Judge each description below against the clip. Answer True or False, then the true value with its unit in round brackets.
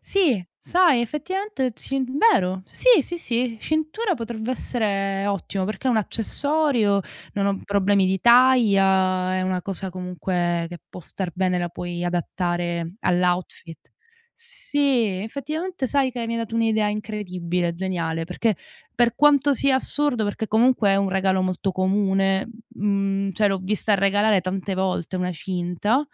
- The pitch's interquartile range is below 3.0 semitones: False (5.0 semitones)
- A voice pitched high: True (200 Hz)